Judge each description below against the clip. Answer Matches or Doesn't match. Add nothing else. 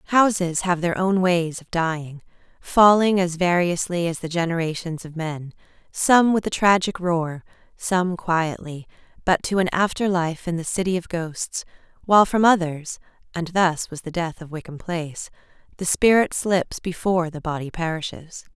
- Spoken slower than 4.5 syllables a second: Doesn't match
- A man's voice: Doesn't match